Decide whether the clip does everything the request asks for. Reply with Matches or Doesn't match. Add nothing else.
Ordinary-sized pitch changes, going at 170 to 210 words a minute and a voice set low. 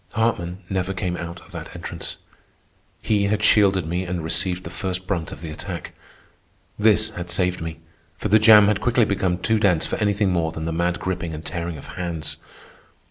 Matches